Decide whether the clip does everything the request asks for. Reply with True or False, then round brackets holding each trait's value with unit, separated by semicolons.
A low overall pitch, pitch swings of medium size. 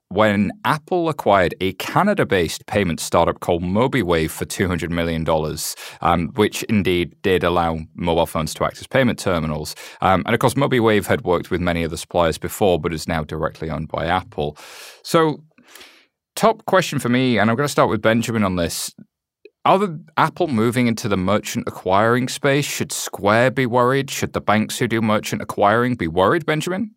False (105 Hz; 7.3 semitones)